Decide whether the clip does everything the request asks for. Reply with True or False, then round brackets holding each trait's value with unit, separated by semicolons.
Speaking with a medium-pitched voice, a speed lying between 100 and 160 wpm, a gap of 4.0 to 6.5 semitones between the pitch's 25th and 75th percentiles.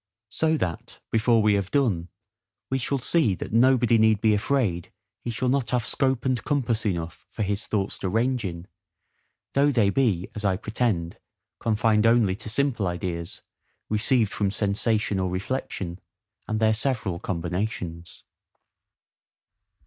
False (110 Hz; 145 wpm; 4.4 semitones)